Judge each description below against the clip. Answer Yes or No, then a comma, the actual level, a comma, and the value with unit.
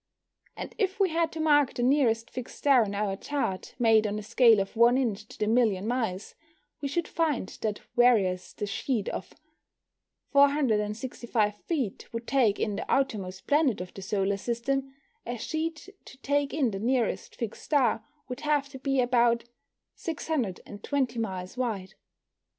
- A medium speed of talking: Yes, average, 160 wpm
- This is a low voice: No, high, 240 Hz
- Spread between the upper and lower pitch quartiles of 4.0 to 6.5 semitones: Yes, average, 4.8 semitones